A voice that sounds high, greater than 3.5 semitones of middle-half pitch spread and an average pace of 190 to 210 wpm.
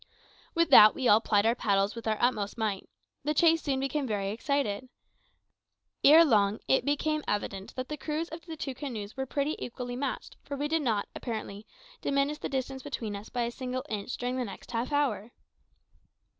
Yes: very high, 255 Hz; average, 4.9 semitones; average, 195 wpm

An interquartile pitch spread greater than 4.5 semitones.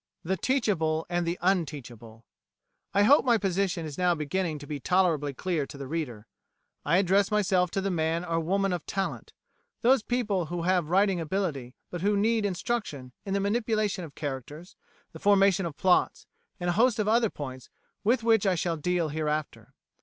No: average, 4.2 semitones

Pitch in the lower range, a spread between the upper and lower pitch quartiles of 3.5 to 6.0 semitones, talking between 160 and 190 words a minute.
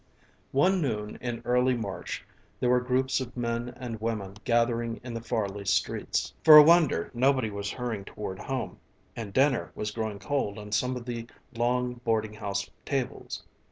No: low, 120 Hz; average, 3.0 semitones; average, 165 wpm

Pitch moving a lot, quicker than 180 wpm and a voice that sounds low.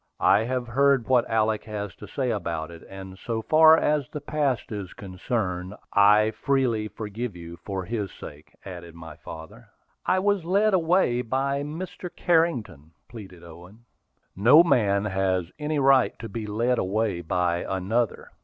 No: wide, 6.3 semitones; average, 155 wpm; low, 110 Hz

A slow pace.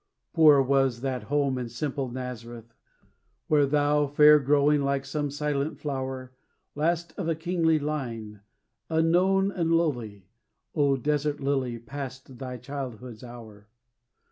Yes: slow, 125 wpm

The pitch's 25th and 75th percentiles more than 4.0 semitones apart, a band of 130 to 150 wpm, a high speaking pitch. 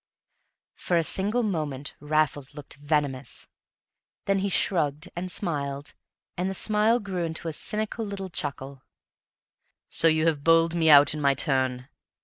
No: average, 4.8 semitones; average, 145 wpm; medium, 160 Hz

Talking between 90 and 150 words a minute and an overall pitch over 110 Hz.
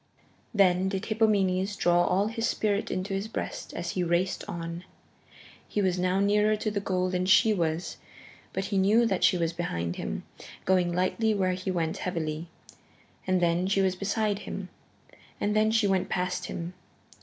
No: average, 175 wpm; high, 190 Hz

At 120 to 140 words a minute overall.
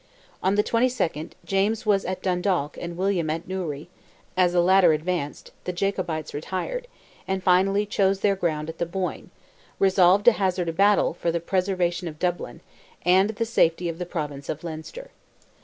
No: average, 170 wpm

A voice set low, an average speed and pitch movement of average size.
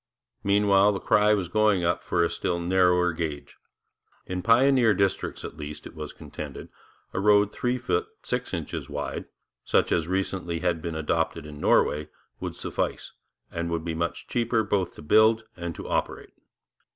Yes: very low, 90 Hz; average, 165 wpm; average, 3.7 semitones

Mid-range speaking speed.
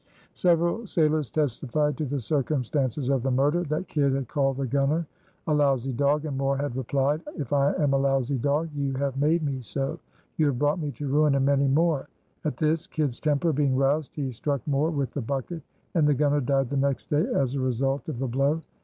No: fast, 215 wpm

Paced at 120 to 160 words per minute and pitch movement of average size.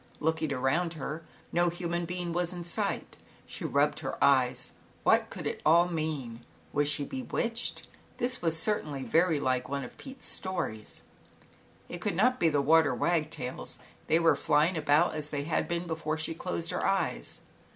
No: average, 170 wpm; average, 3.3 semitones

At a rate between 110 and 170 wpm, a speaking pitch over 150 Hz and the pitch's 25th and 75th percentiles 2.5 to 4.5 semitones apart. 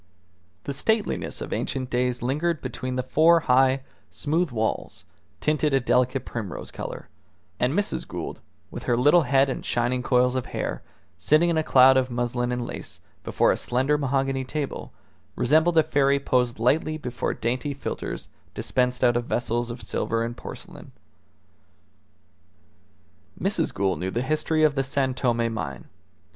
No: average, 155 wpm; low, 130 Hz; average, 3.0 semitones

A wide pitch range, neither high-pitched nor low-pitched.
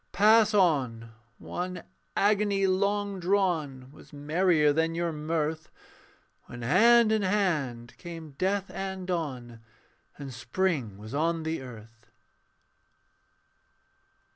Yes: wide, 5.8 semitones; medium, 165 Hz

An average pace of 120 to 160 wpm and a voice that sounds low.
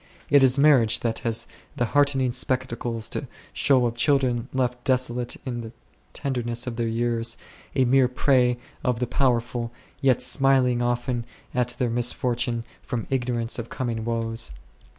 Yes: average, 150 wpm; low, 120 Hz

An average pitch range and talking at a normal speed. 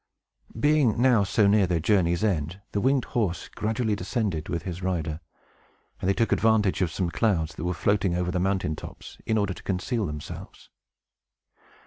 Yes: average, 4.0 semitones; average, 170 wpm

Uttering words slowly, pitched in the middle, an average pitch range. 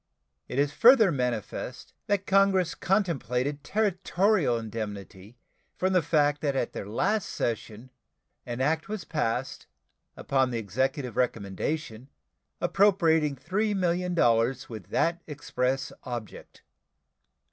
No: slow, 105 wpm; medium, 145 Hz; wide, 7.1 semitones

